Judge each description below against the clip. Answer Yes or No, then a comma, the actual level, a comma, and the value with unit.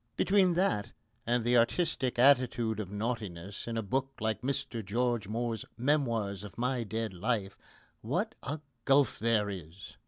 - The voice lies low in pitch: Yes, low, 115 Hz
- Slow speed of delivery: No, average, 150 wpm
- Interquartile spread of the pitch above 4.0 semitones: No, average, 3.7 semitones